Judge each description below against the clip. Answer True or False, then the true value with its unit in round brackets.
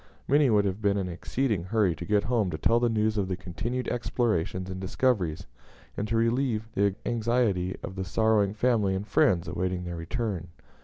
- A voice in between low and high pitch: False (100 Hz)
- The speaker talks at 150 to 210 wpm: True (190 wpm)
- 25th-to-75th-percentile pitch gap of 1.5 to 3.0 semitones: False (3.9 semitones)